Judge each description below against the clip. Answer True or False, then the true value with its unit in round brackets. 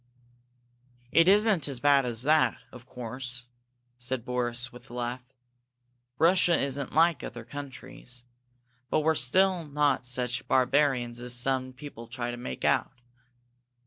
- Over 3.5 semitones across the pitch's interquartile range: False (3.1 semitones)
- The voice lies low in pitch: True (130 Hz)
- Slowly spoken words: True (130 wpm)